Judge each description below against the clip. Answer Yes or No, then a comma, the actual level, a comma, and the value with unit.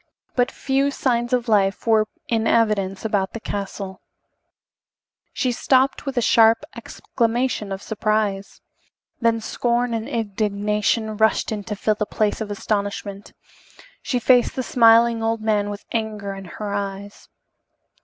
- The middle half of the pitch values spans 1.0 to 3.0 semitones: Yes, narrow, 2.5 semitones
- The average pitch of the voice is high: Yes, high, 220 Hz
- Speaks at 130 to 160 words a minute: Yes, average, 140 wpm